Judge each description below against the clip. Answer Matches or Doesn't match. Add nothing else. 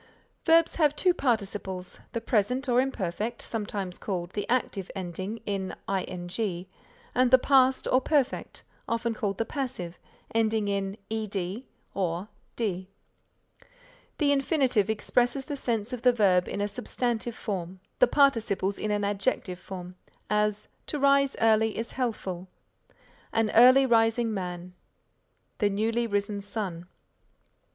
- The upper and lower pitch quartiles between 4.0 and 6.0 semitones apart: Matches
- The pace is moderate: Doesn't match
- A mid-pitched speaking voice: Doesn't match